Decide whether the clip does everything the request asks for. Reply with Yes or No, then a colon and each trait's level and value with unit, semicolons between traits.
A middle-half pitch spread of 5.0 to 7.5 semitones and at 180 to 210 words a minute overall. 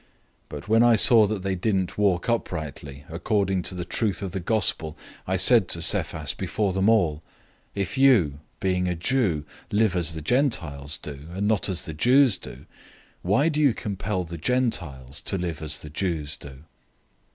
Yes: wide, 5.5 semitones; average, 185 wpm